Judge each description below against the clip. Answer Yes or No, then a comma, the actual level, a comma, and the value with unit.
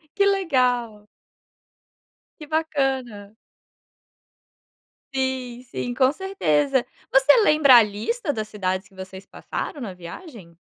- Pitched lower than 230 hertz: No, very high, 255 Hz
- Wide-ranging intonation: Yes, wide, 5.9 semitones